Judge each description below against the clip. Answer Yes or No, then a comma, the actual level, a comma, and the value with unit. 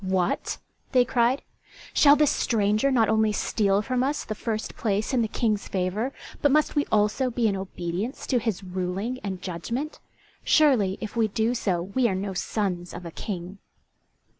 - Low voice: No, high, 215 Hz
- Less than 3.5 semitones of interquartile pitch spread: No, average, 4.5 semitones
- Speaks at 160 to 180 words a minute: Yes, average, 175 wpm